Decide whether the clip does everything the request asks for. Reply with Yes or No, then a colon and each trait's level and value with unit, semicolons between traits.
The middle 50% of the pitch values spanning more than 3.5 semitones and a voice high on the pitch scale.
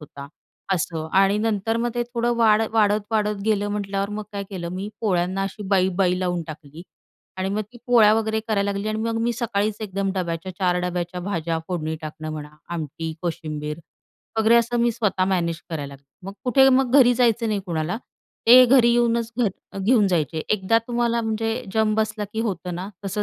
Yes: average, 4.1 semitones; high, 200 Hz